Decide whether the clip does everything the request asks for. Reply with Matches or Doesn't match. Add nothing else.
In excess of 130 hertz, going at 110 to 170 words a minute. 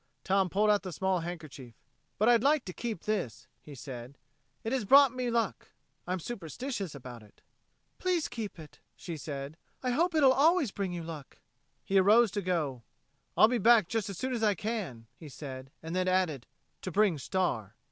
Doesn't match